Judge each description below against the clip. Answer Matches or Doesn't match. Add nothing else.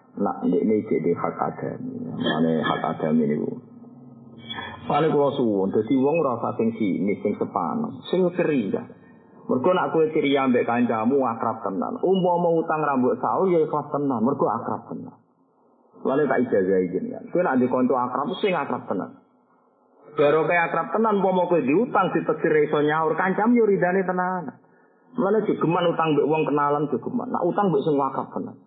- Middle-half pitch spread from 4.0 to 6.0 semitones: Matches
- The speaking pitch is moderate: Matches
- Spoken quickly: Matches